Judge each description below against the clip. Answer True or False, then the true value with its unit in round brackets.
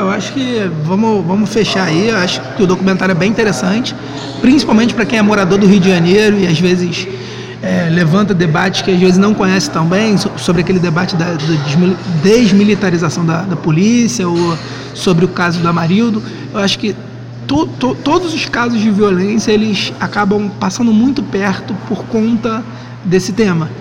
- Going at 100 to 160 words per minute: False (175 wpm)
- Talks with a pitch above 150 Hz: True (190 Hz)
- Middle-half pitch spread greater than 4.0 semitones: False (3.4 semitones)